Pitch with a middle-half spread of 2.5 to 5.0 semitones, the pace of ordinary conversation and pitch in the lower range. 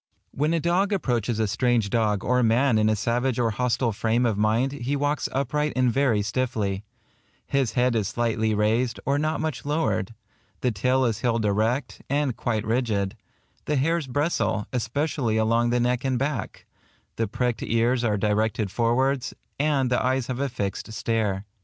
Yes: average, 3.4 semitones; average, 180 wpm; low, 120 Hz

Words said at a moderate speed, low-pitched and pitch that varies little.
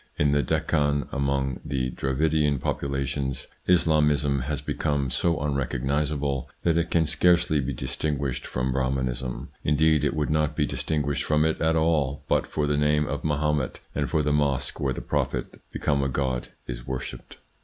Yes: average, 165 wpm; very low, 70 Hz; narrow, 2.1 semitones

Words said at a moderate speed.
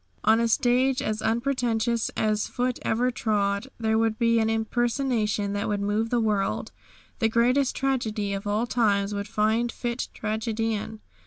Yes: average, 155 wpm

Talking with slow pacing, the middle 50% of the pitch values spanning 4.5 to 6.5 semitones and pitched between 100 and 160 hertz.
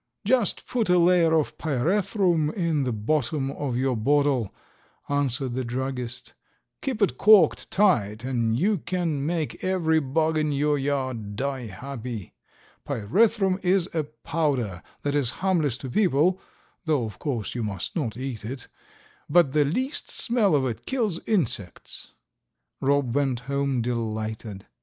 No: average, 145 wpm; wide, 5.6 semitones; medium, 140 Hz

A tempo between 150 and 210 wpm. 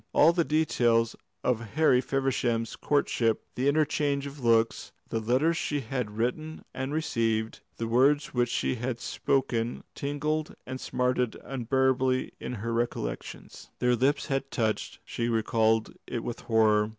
No: average, 140 wpm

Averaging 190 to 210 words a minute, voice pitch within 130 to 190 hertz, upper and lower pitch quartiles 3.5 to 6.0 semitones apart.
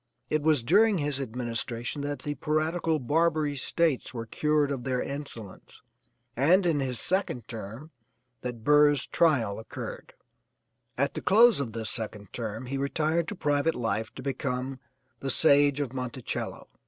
No: average, 150 wpm; medium, 140 Hz; average, 4.0 semitones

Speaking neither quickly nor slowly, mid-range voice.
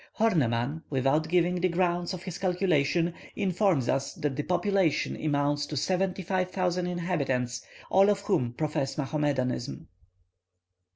No: slow, 130 wpm; medium, 170 Hz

